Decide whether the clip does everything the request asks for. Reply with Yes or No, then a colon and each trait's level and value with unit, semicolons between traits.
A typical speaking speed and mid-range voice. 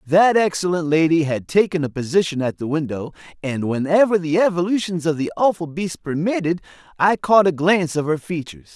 Yes: average, 180 wpm; medium, 165 Hz